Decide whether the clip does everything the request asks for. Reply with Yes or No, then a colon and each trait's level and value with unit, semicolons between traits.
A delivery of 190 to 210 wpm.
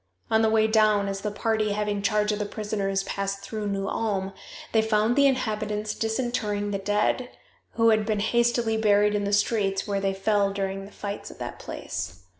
Yes: average, 195 wpm